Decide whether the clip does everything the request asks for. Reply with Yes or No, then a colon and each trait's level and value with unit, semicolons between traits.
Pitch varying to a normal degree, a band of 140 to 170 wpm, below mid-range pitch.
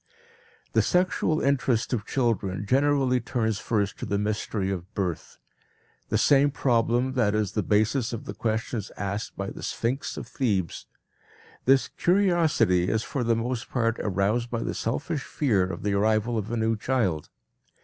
Yes: average, 4.0 semitones; average, 160 wpm; low, 115 Hz